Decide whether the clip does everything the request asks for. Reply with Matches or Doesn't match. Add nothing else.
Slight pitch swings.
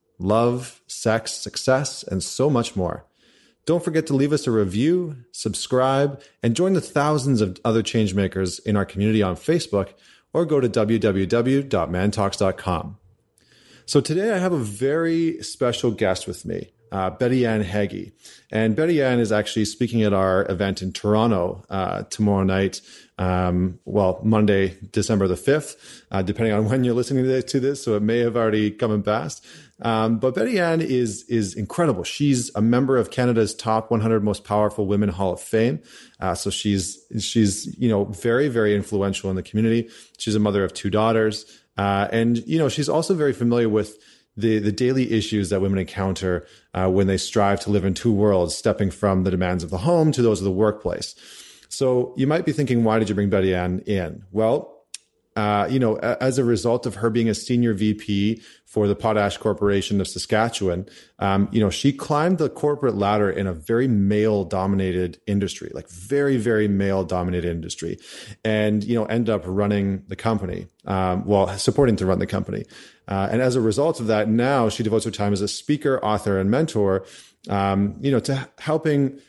Doesn't match